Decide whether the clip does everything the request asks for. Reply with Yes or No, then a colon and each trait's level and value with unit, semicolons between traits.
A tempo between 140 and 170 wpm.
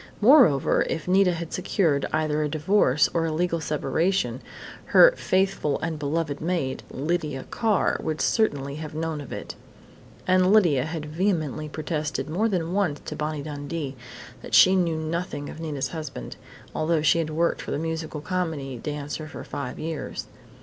Yes: average, 160 wpm